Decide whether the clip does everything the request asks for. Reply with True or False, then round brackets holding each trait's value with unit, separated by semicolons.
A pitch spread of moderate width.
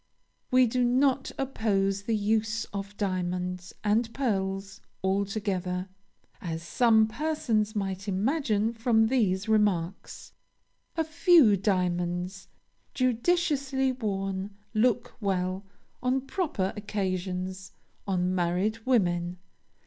True (4.4 semitones)